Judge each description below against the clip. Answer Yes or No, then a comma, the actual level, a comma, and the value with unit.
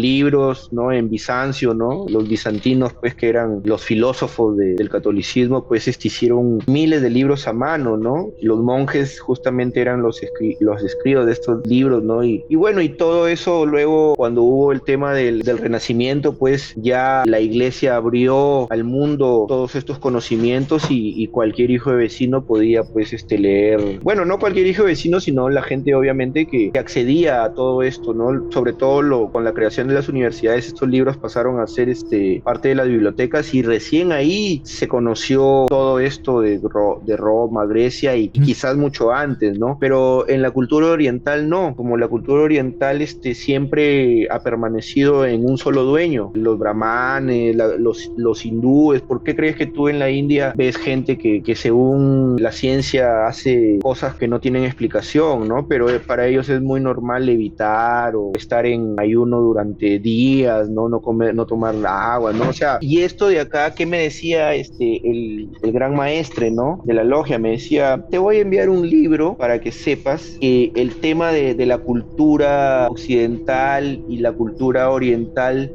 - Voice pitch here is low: Yes, low, 130 Hz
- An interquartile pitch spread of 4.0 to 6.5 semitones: No, average, 3.4 semitones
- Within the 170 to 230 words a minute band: Yes, average, 185 wpm